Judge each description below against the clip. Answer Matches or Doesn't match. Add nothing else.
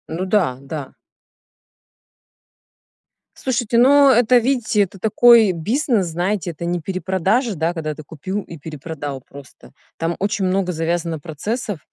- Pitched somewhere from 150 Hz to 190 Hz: Matches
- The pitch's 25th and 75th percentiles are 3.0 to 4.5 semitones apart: Doesn't match